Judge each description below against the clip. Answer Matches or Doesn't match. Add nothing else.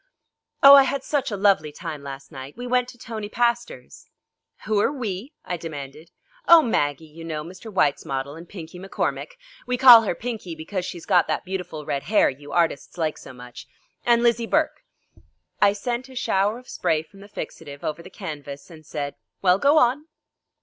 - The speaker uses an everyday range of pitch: Doesn't match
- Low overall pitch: Doesn't match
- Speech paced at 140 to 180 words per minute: Doesn't match